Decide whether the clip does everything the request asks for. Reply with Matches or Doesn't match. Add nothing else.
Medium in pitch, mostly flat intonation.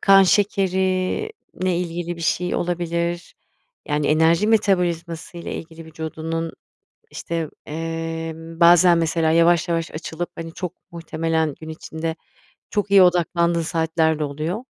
Matches